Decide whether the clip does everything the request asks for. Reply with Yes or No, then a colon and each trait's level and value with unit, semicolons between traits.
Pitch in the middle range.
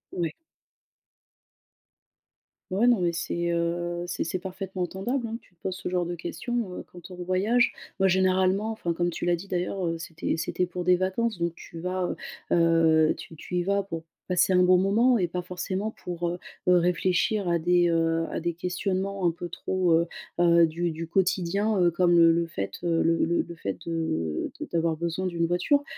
Yes: medium, 175 Hz